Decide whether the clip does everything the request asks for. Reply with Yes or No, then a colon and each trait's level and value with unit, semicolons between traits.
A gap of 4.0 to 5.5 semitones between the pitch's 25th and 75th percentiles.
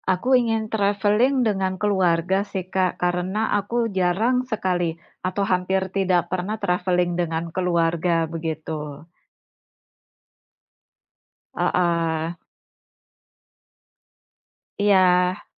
No: average, 2.8 semitones